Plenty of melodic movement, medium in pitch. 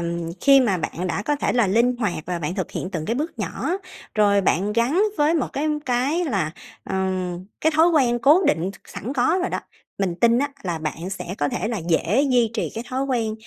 No: wide, 6.8 semitones; high, 225 Hz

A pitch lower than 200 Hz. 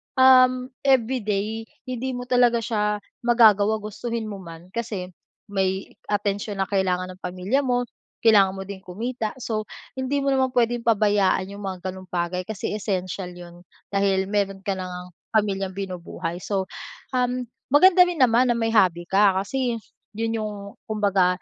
No: high, 205 Hz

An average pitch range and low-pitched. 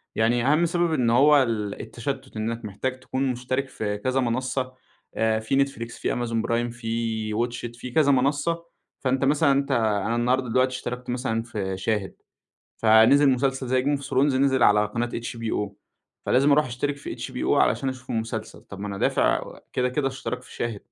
Yes: average, 3.0 semitones; low, 125 Hz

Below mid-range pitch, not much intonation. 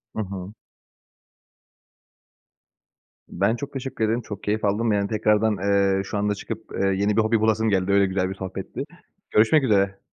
Yes: low, 105 Hz; narrow, 2.1 semitones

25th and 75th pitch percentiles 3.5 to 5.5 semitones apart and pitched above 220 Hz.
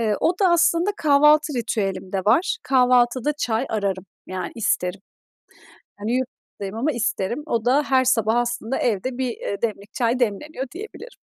Yes: average, 5.2 semitones; high, 240 Hz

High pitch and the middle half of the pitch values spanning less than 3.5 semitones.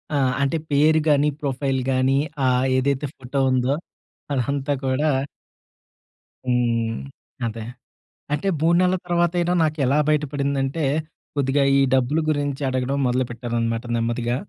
No: low, 135 Hz; average, 2.8 semitones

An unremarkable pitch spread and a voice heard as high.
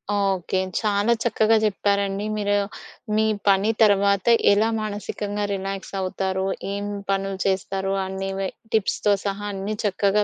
No: narrow, 1.2 semitones; high, 200 Hz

